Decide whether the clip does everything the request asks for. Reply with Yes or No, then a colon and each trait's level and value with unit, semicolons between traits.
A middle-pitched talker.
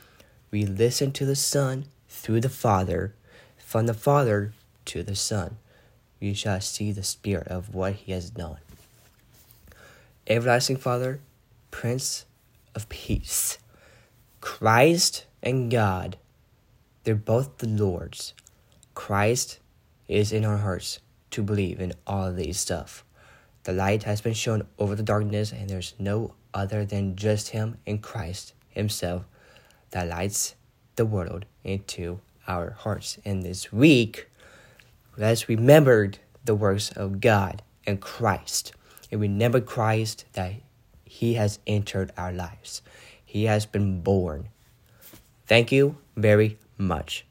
No: low, 105 Hz